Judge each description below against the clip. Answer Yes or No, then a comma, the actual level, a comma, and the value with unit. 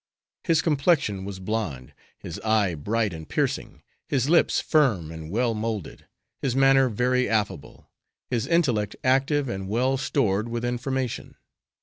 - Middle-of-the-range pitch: No, low, 115 Hz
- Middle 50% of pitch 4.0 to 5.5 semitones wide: Yes, average, 5.1 semitones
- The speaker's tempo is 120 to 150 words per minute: Yes, slow, 135 wpm